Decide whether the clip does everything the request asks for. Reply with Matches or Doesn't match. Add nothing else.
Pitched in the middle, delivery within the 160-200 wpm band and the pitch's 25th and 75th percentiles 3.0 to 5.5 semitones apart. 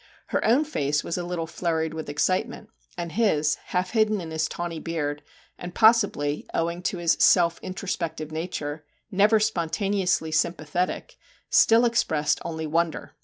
Doesn't match